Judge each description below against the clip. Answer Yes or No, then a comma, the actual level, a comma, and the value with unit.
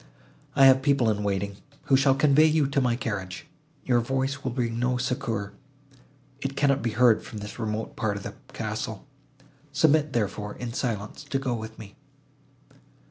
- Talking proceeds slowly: No, average, 170 wpm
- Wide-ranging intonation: No, average, 4.0 semitones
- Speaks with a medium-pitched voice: No, low, 125 Hz